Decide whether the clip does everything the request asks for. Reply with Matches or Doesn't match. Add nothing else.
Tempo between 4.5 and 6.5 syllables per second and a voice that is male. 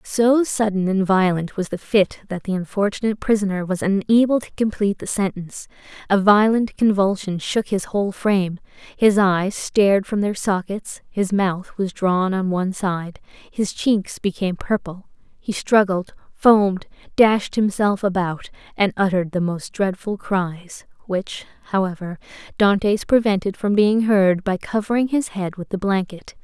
Doesn't match